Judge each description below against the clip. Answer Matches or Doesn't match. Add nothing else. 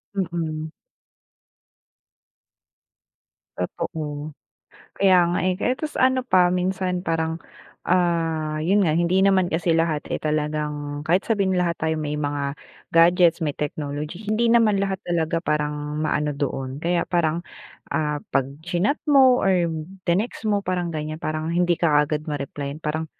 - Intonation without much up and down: Doesn't match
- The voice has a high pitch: Doesn't match